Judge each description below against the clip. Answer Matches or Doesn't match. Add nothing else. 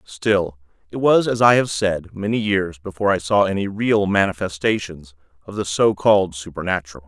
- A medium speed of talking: Matches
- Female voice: Doesn't match